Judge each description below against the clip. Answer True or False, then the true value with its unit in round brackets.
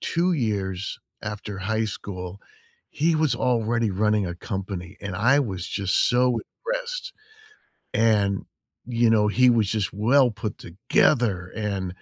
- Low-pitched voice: True (105 Hz)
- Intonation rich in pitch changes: False (3.9 semitones)